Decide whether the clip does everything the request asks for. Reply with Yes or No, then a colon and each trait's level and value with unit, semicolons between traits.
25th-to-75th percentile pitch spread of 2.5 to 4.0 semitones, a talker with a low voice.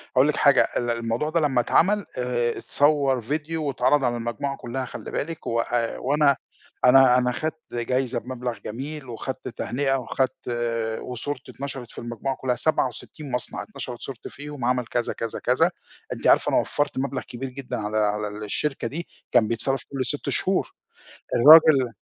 Yes: average, 3.0 semitones; low, 130 Hz